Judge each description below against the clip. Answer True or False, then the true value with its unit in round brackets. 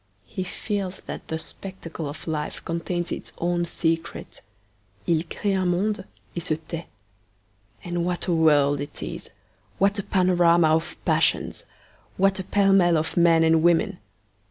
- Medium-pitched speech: True (175 Hz)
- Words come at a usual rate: True (155 wpm)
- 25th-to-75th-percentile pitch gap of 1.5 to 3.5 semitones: True (2.5 semitones)